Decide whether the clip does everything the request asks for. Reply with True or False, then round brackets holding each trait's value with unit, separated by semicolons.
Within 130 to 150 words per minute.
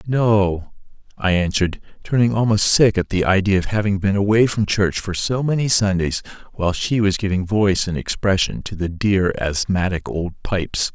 False (175 wpm)